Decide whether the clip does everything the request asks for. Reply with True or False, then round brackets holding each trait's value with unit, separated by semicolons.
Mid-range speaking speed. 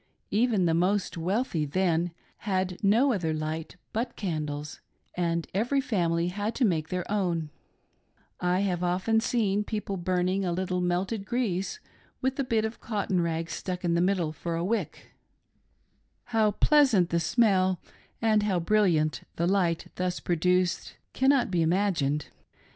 True (150 wpm)